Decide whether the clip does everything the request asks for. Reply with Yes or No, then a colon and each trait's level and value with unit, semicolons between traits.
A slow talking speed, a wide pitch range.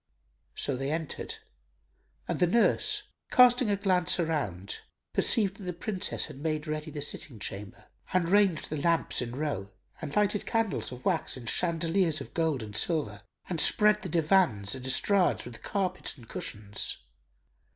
No: average, 160 wpm; wide, 6.3 semitones